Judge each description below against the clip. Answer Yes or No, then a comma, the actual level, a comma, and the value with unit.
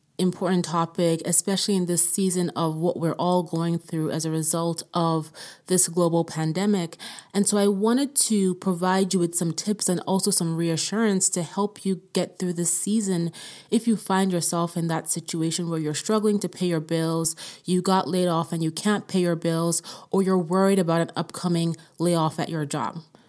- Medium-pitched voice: Yes, medium, 175 Hz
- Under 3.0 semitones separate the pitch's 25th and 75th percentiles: Yes, narrow, 2.4 semitones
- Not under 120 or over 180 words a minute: No, average, 190 wpm